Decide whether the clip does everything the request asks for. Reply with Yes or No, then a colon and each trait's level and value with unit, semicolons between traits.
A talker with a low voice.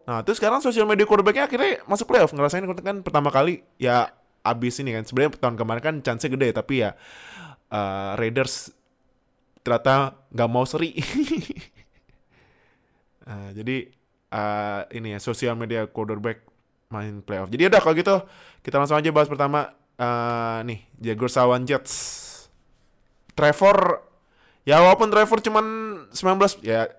Yes: low, 130 Hz